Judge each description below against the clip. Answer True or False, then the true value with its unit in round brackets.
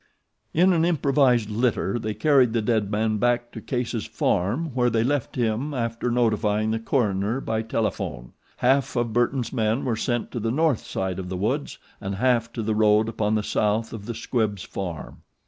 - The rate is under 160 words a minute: False (185 wpm)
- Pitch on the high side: False (115 Hz)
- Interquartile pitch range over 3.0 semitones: False (2.7 semitones)